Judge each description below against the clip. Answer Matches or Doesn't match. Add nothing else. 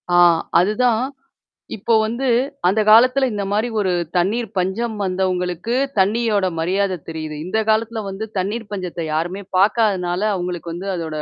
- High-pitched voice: Matches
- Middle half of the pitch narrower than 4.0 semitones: Matches